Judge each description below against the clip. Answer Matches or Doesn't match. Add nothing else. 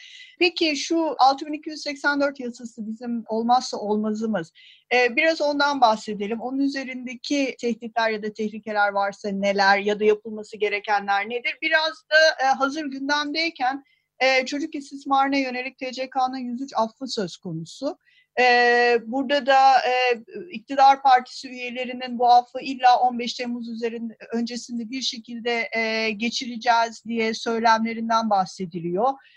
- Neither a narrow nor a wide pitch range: Matches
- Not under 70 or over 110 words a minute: Doesn't match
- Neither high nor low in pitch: Doesn't match